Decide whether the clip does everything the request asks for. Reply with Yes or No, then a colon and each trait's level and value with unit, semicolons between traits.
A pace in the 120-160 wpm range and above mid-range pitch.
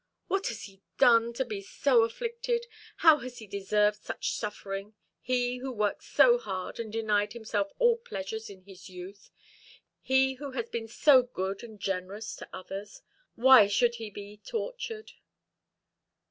Yes: average, 155 wpm; high, 225 Hz